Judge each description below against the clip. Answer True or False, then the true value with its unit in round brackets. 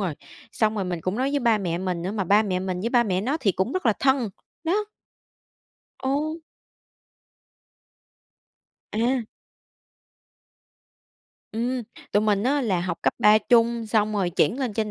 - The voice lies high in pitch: True (215 Hz)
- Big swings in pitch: False (4.6 semitones)